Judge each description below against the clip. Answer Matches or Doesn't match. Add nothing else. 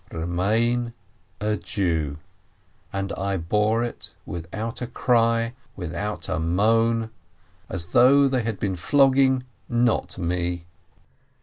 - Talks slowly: Matches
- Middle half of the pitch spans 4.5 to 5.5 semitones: Matches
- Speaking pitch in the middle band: Doesn't match